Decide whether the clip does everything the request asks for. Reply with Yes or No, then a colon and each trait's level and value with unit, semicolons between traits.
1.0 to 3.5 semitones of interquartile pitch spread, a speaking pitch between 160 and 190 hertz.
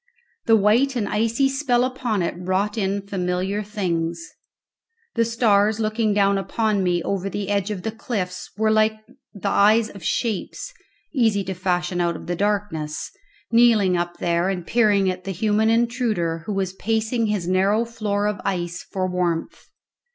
No: average, 3.2 semitones; high, 200 Hz